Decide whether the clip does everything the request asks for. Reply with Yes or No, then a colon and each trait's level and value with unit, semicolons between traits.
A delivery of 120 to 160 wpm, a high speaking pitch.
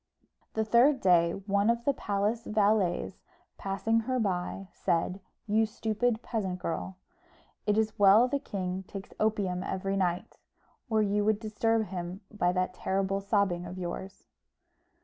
Yes: average, 145 wpm; high, 200 Hz